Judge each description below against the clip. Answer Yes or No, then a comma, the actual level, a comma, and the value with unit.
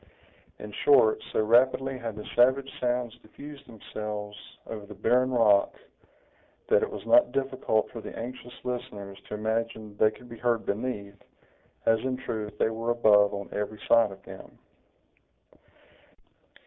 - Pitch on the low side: Yes, low, 115 Hz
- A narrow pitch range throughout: No, average, 3.1 semitones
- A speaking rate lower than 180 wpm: Yes, average, 150 wpm